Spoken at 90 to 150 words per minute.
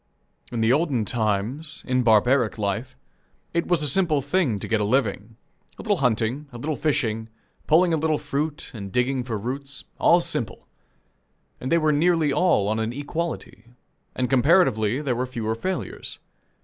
No: average, 165 wpm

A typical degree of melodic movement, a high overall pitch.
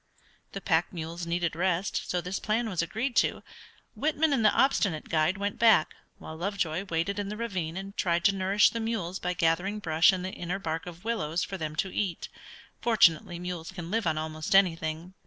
No: average, 3.5 semitones; medium, 180 Hz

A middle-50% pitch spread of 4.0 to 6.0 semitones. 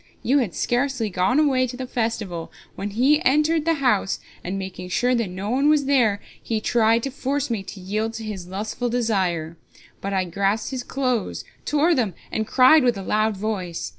Yes: average, 4.9 semitones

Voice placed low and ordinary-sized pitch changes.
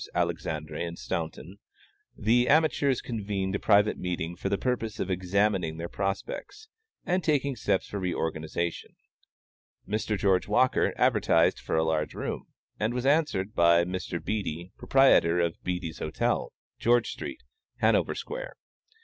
No: very low, 95 Hz; wide, 6.0 semitones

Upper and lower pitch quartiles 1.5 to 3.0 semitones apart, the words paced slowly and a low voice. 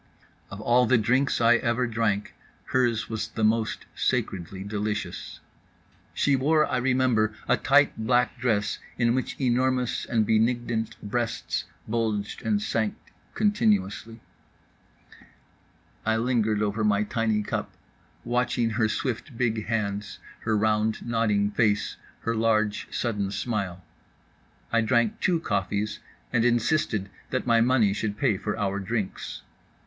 Yes: narrow, 2.6 semitones; slow, 130 wpm; low, 115 Hz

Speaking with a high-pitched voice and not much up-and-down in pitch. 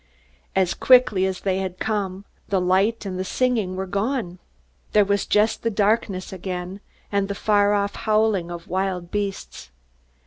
Yes: high, 195 Hz; narrow, 2.2 semitones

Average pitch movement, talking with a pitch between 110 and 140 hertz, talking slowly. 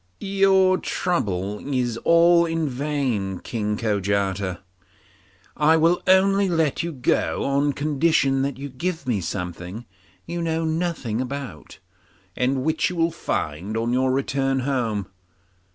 No: wide, 7.0 semitones; low, 135 Hz; slow, 130 wpm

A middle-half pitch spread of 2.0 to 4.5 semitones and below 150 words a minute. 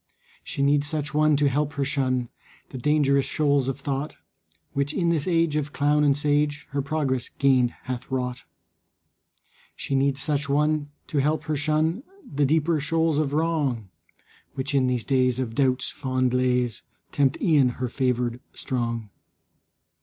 No: average, 2.7 semitones; average, 155 wpm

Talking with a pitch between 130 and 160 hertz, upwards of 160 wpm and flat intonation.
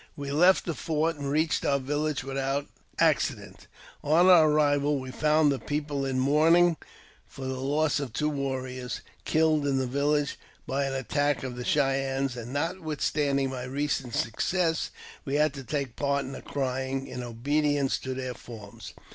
Yes: medium, 140 Hz; average, 170 wpm; narrow, 2.3 semitones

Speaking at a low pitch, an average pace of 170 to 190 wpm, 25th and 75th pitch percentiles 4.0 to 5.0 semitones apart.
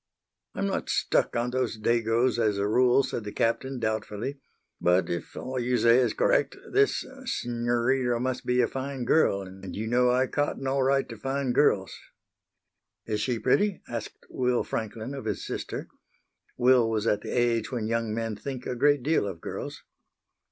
No: low, 120 Hz; average, 175 wpm; average, 2.8 semitones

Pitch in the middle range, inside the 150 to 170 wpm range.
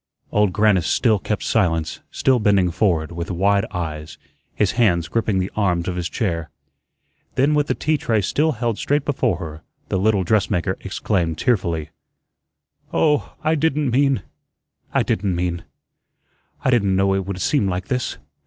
No: low, 100 Hz; average, 160 wpm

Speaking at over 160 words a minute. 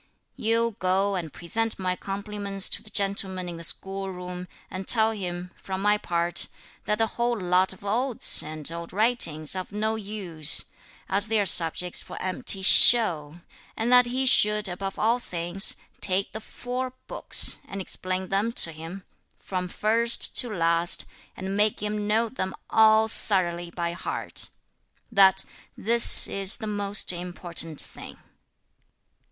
No: average, 150 wpm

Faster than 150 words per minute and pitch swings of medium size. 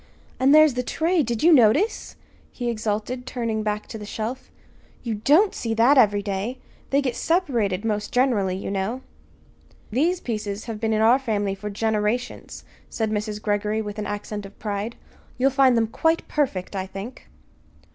Yes: average, 170 wpm; average, 3.6 semitones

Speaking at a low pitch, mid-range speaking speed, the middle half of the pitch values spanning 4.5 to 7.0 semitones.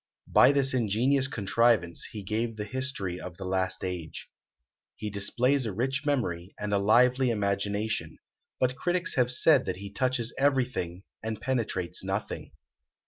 Yes: low, 110 Hz; average, 145 wpm; average, 4.8 semitones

